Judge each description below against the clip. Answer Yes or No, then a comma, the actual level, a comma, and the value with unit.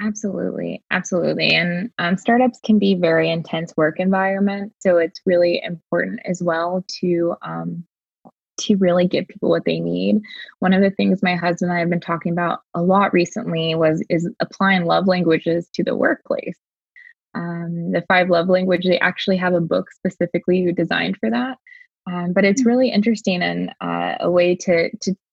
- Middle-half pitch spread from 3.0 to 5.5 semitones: No, narrow, 2.4 semitones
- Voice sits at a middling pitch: Yes, medium, 180 Hz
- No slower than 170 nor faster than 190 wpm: Yes, average, 180 wpm